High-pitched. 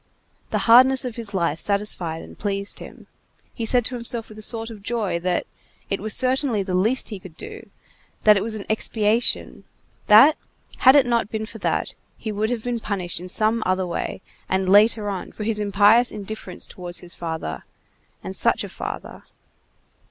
Yes: high, 210 Hz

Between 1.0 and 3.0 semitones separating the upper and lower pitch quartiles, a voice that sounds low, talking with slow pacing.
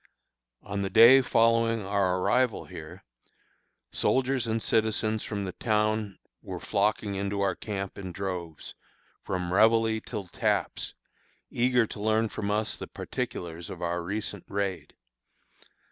Yes: narrow, 2.6 semitones; low, 105 Hz; slow, 130 wpm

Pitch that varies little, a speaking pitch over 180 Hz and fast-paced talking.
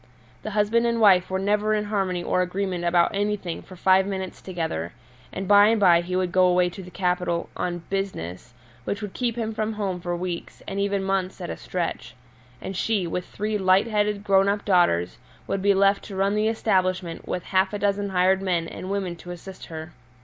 Yes: narrow, 2.2 semitones; high, 190 Hz; fast, 210 wpm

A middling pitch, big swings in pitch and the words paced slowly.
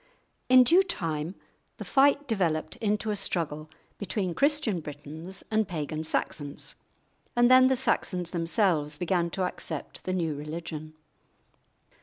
Yes: medium, 175 Hz; wide, 5.9 semitones; slow, 130 wpm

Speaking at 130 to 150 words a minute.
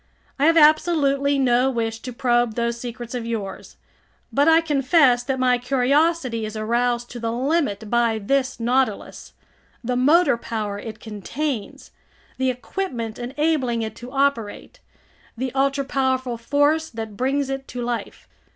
Yes: average, 145 wpm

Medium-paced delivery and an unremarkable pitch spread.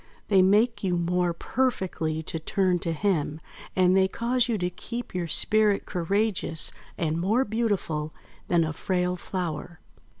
Yes: average, 145 wpm; average, 3.8 semitones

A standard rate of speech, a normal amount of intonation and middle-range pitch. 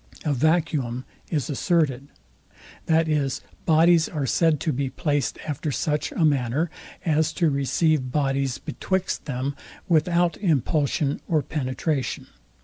No: slow, 125 wpm; average, 3.0 semitones; medium, 150 Hz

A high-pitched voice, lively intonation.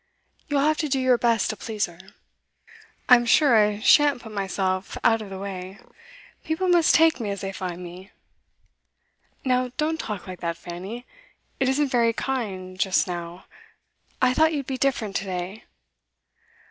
Yes: high, 220 Hz; wide, 5.9 semitones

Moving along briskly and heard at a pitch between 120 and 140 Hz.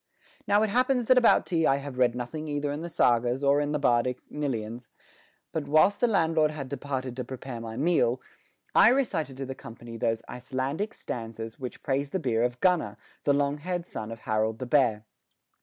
No: average, 195 wpm; low, 135 Hz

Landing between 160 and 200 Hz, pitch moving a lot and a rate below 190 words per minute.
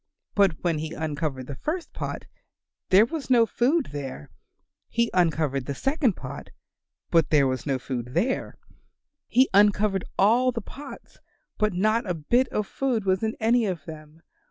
Yes: high, 190 Hz; wide, 7.5 semitones; average, 160 wpm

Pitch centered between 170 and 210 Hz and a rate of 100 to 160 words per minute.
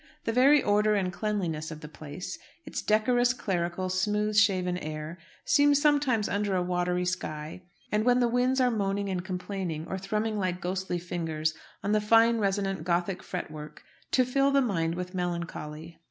No: high, 190 Hz; average, 170 wpm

